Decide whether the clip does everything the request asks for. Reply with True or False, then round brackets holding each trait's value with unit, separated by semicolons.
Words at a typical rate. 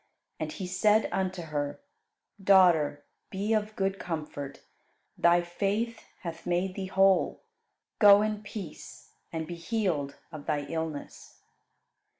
False (125 wpm)